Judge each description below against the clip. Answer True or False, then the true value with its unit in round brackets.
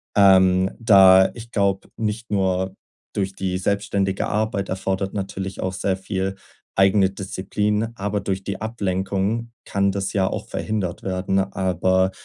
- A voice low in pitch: True (95 Hz)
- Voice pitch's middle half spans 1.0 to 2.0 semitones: True (1.3 semitones)